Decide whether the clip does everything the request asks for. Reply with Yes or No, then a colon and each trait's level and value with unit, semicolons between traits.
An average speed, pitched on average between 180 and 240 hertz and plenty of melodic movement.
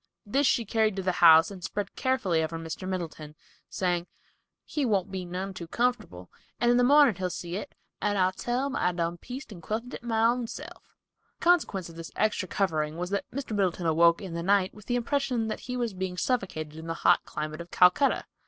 No: fast, 220 wpm; high, 190 Hz; wide, 5.7 semitones